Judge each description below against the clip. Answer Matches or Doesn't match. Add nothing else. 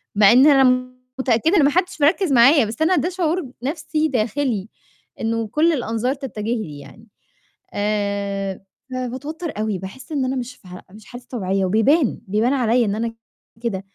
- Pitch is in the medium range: Doesn't match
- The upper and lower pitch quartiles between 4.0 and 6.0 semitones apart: Matches